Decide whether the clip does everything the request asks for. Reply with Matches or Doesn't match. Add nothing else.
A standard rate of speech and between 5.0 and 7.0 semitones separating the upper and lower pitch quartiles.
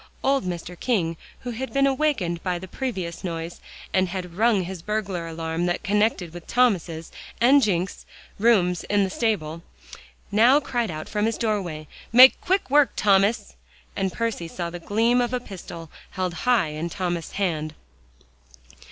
Matches